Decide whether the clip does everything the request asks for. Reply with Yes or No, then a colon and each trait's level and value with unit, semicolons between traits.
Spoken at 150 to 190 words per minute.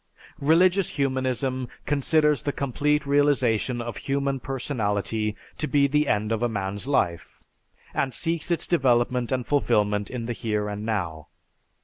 No: average, 140 wpm